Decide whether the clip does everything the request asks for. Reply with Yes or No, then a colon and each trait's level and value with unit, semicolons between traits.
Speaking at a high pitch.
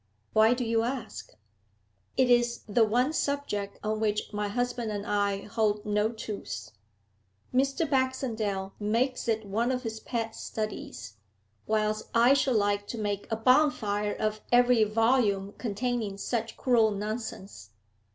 Yes: high, 220 Hz